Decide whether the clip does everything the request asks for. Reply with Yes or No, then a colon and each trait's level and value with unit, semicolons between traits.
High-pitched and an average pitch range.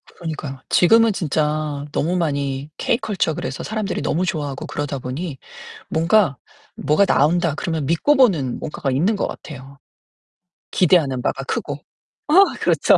No: medium, 155 Hz; average, 4.4 semitones